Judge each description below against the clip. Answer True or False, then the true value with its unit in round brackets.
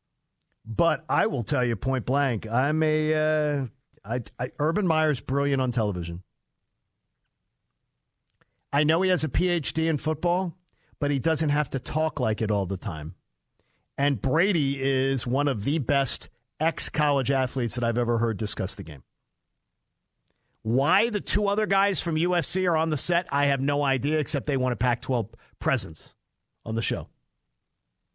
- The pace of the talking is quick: False (165 wpm)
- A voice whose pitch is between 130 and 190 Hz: True (140 Hz)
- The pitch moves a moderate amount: True (4.5 semitones)